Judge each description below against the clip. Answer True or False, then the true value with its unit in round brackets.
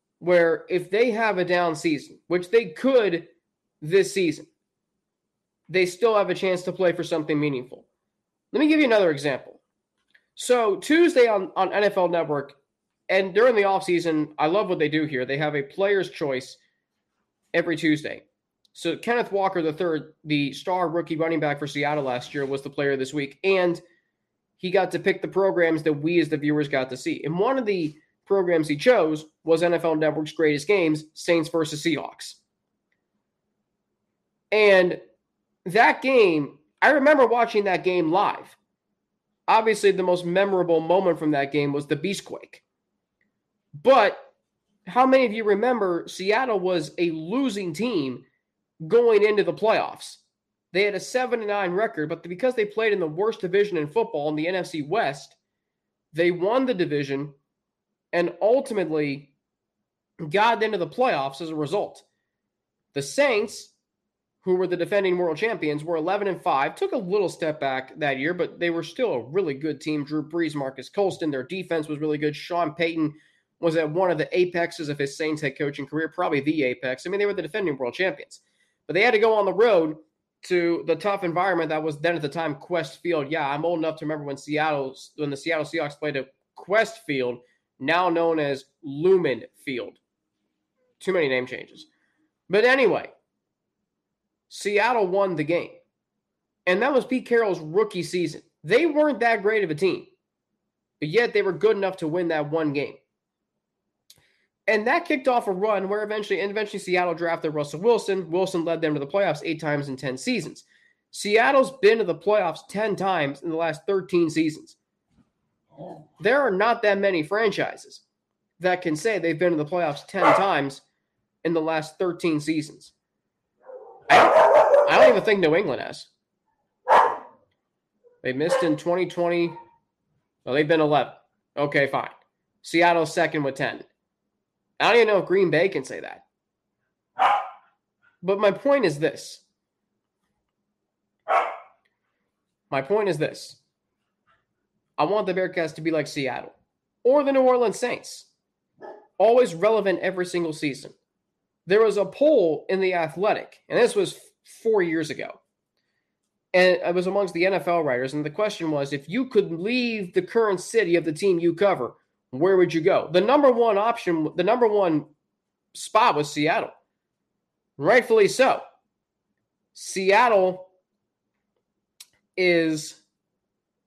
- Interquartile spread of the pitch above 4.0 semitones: True (5.1 semitones)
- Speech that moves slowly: False (165 wpm)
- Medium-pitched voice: True (175 Hz)